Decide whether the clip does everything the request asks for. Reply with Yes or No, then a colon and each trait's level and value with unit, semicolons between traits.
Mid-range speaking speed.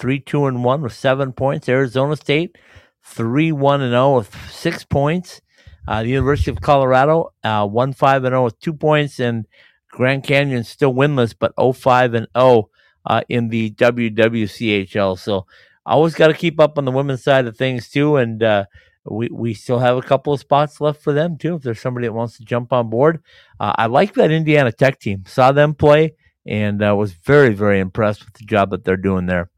No: fast, 215 wpm